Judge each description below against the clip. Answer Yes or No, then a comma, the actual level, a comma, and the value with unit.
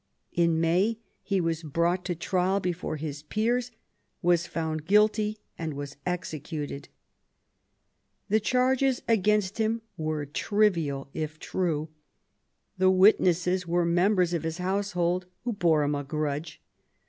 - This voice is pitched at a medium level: Yes, medium, 175 Hz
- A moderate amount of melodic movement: Yes, average, 4.2 semitones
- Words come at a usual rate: No, slow, 125 wpm